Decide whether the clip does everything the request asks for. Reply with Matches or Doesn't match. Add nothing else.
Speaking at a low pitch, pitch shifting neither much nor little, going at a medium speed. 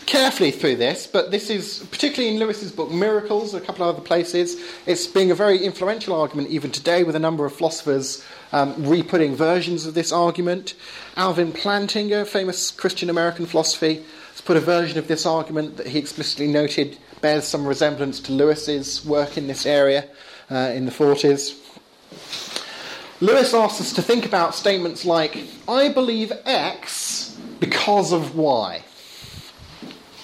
Doesn't match